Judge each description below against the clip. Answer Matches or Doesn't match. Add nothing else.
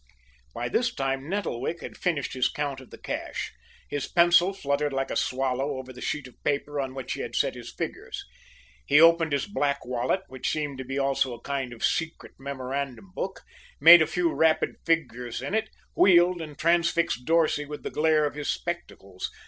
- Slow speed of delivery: Doesn't match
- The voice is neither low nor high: Matches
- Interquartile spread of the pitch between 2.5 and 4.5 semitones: Matches